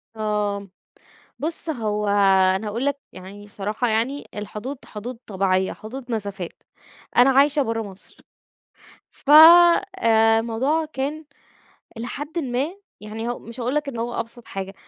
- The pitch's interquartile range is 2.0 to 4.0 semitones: No, average, 4.7 semitones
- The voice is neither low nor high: No, high, 230 Hz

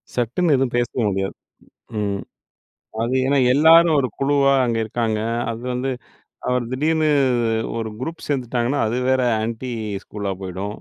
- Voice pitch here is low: Yes, low, 125 Hz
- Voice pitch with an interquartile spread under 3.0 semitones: No, average, 3.8 semitones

